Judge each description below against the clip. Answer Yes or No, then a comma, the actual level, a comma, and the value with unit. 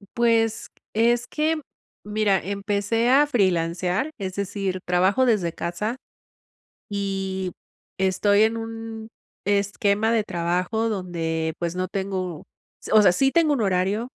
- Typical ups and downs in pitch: Yes, average, 3.5 semitones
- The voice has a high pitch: Yes, high, 200 Hz